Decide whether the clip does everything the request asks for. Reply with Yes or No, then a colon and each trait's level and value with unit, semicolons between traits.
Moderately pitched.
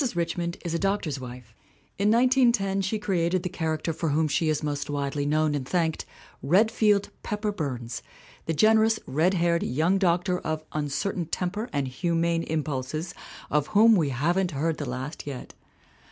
Yes: medium, 165 Hz